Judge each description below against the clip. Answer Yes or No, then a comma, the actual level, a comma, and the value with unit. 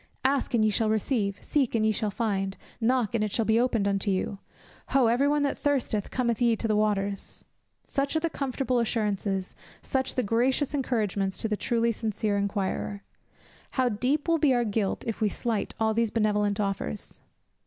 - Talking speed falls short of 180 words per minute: No, average, 185 wpm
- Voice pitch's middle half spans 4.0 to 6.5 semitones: No, average, 3.6 semitones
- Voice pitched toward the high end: Yes, high, 225 Hz